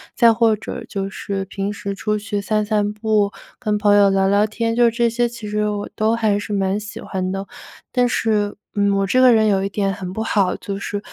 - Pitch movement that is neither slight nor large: No, narrow, 1.8 semitones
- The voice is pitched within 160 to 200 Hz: No, high, 210 Hz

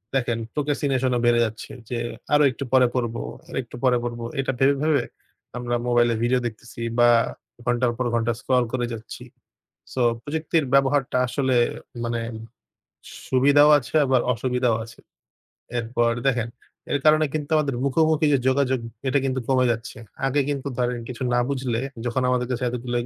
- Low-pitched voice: Yes, low, 125 Hz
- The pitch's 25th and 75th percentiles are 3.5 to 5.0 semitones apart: No, narrow, 2.5 semitones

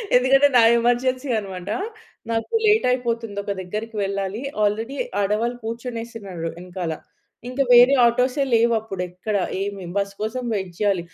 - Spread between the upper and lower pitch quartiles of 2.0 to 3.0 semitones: No, average, 3.7 semitones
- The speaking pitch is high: Yes, high, 225 Hz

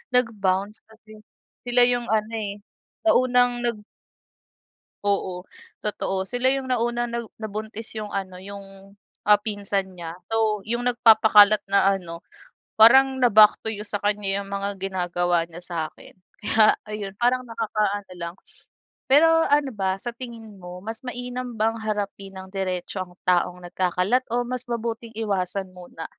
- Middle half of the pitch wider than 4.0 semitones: No, average, 3.4 semitones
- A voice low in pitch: No, high, 210 Hz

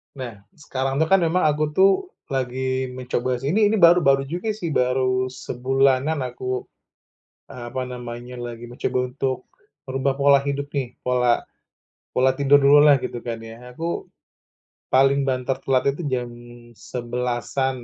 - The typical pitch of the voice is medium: No, low, 130 Hz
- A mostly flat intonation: Yes, narrow, 2.0 semitones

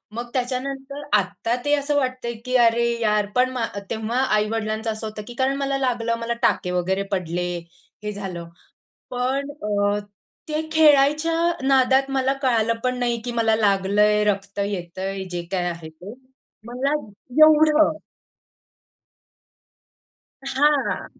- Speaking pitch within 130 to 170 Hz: No, high, 235 Hz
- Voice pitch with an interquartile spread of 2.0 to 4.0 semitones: No, average, 4.8 semitones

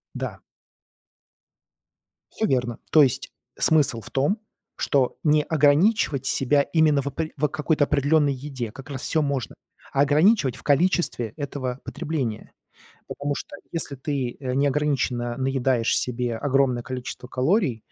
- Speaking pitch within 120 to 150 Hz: Yes, medium, 140 Hz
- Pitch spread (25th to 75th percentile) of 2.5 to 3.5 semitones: Yes, average, 2.8 semitones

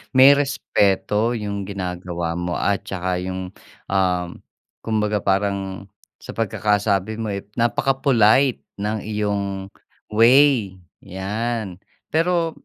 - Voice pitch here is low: Yes, low, 100 Hz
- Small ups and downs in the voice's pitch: No, average, 3.0 semitones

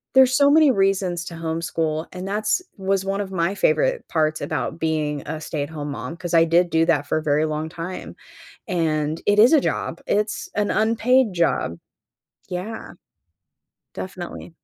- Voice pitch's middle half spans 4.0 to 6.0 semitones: Yes, average, 4.4 semitones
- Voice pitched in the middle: Yes, medium, 175 Hz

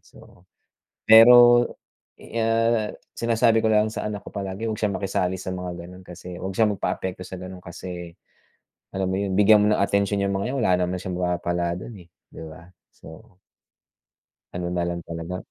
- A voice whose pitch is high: No, very low, 95 Hz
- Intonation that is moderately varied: Yes, average, 3.0 semitones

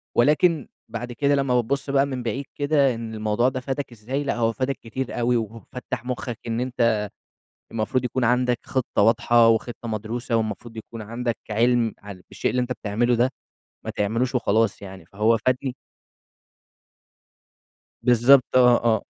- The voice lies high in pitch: No, low, 120 Hz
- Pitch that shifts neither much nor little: No, narrow, 2.2 semitones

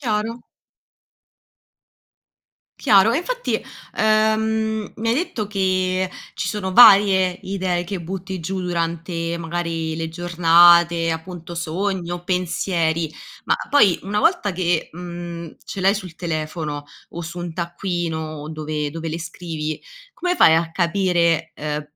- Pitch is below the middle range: No, medium, 175 Hz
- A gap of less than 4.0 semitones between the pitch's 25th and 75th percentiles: Yes, average, 2.8 semitones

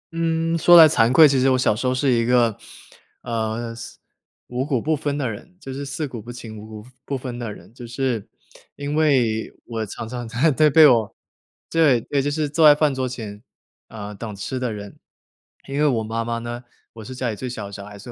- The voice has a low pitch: Yes, low, 125 Hz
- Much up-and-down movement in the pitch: No, average, 4.0 semitones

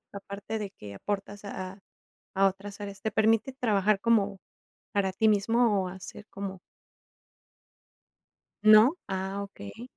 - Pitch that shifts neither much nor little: No, narrow, 1.9 semitones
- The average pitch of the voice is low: No, high, 200 Hz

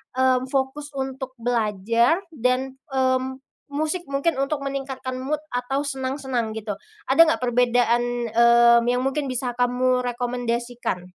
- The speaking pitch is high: Yes, very high, 255 Hz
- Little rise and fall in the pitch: Yes, narrow, 2.0 semitones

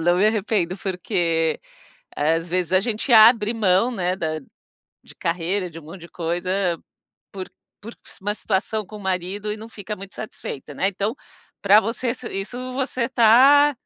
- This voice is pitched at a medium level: No, high, 195 Hz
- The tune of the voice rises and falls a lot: No, average, 3.9 semitones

